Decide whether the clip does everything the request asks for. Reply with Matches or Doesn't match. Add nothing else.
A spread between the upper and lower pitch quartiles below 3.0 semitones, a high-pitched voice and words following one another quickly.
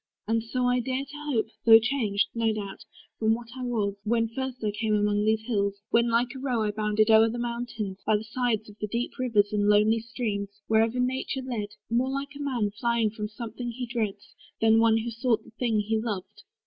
Matches